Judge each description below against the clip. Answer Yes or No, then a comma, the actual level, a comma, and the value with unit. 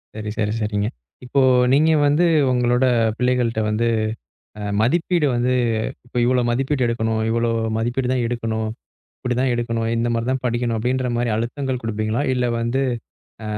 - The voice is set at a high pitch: No, low, 120 Hz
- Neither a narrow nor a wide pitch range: No, narrow, 2.0 semitones